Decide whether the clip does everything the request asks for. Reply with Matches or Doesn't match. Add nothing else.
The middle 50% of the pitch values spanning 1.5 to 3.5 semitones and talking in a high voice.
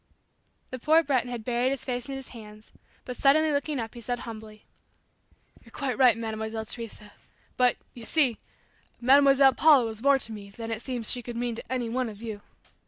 Matches